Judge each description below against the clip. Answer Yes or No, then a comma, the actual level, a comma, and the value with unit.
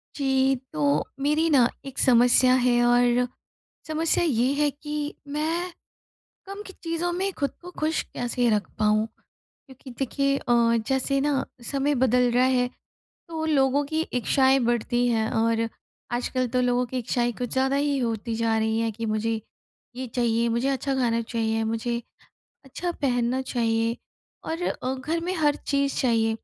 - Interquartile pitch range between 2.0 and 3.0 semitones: No, average, 3.4 semitones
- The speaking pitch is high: Yes, very high, 255 Hz